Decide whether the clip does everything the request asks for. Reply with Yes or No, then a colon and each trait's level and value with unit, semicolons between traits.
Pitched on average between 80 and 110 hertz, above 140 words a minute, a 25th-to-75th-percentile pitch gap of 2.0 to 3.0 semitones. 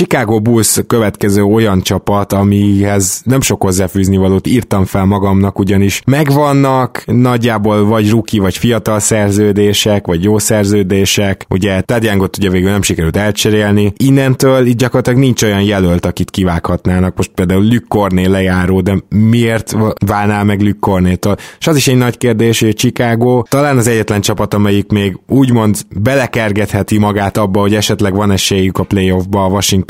Yes: low, 105 Hz; average, 150 wpm; average, 2.7 semitones